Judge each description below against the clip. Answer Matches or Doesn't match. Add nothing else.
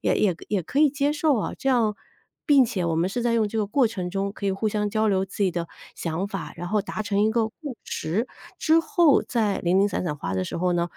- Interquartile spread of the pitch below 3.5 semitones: Doesn't match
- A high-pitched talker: Matches